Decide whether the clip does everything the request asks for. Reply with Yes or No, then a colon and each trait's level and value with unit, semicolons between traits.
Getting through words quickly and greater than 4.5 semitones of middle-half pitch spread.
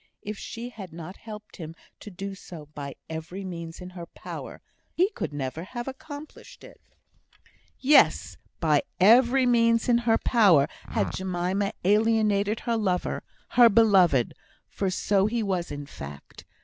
No: average, 150 wpm; average, 5.0 semitones